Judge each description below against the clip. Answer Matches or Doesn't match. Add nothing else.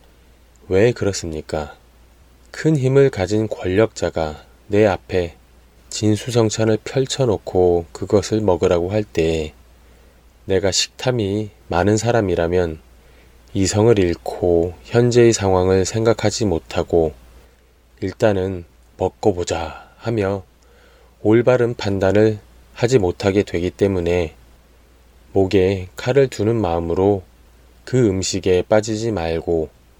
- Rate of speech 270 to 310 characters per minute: Doesn't match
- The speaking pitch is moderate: Doesn't match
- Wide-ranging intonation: Matches